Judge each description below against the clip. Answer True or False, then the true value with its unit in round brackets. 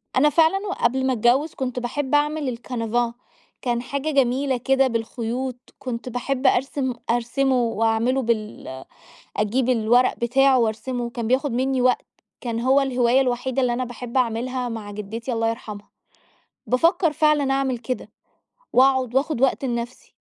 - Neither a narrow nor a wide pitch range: False (2.3 semitones)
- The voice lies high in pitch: True (250 Hz)